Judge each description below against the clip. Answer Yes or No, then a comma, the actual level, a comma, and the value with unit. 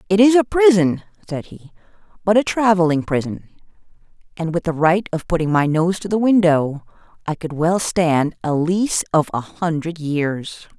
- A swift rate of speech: No, average, 170 wpm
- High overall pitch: No, medium, 170 Hz